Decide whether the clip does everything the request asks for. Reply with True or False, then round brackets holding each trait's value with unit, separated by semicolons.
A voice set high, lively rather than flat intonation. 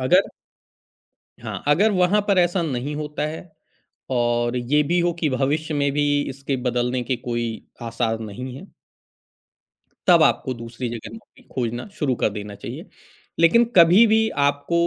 False (140 Hz; 5.8 semitones)